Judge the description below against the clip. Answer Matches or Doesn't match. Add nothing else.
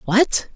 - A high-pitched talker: Matches